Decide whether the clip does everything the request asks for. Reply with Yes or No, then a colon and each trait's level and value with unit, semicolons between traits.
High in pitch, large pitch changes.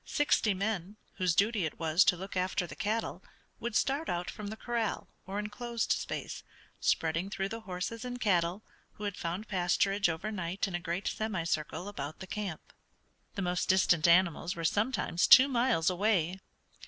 No: high, 195 Hz; average, 3.7 semitones